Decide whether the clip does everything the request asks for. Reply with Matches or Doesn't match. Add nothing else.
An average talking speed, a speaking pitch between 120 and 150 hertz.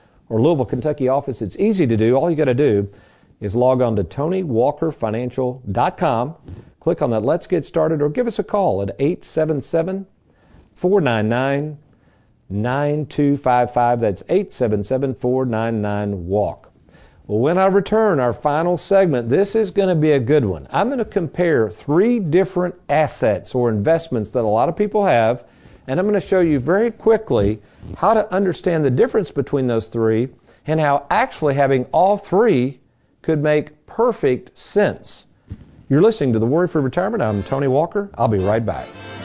Matches